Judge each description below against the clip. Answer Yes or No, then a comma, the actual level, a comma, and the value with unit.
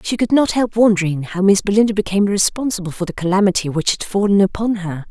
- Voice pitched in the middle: No, high, 200 Hz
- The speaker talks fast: Yes, fast, 210 wpm